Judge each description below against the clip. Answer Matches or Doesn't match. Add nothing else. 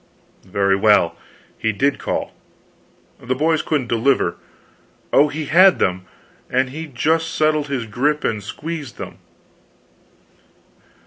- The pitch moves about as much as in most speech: Doesn't match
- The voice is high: Doesn't match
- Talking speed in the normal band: Doesn't match